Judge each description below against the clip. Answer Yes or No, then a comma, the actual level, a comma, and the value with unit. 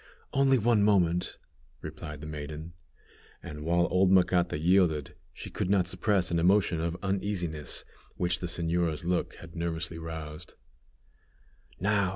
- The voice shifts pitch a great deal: No, average, 2.7 semitones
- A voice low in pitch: Yes, very low, 85 Hz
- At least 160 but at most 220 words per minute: No, slow, 135 wpm